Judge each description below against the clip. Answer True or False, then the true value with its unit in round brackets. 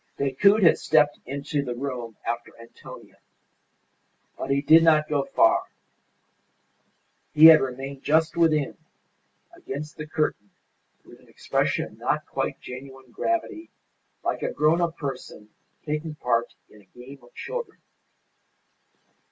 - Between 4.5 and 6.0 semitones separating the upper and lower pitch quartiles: False (3.7 semitones)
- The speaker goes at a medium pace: False (130 wpm)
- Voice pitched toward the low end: False (145 Hz)